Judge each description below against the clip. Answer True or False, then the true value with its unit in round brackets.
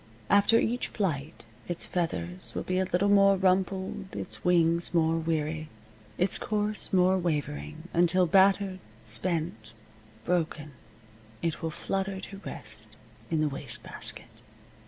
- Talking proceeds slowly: True (130 wpm)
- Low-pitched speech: False (175 Hz)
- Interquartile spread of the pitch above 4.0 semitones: False (3.3 semitones)